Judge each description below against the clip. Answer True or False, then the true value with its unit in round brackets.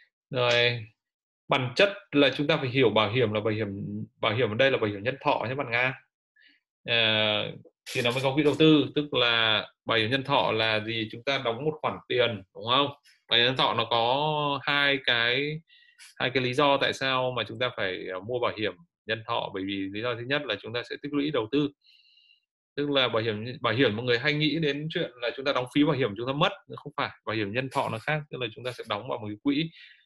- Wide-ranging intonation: False (4.2 semitones)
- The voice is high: False (130 Hz)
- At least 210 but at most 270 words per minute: True (250 wpm)